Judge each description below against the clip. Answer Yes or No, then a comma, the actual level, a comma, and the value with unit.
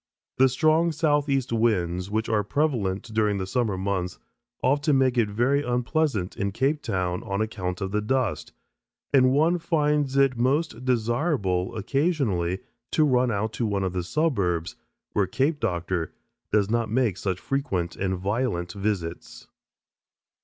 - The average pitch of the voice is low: Yes, low, 110 Hz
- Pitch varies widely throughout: Yes, wide, 6.3 semitones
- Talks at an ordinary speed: Yes, average, 145 wpm